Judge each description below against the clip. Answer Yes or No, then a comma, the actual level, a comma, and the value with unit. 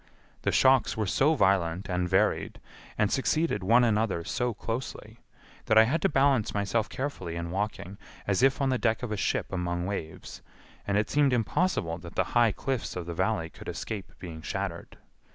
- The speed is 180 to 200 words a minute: Yes, average, 185 wpm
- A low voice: Yes, low, 105 Hz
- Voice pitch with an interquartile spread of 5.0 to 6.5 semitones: Yes, wide, 5.5 semitones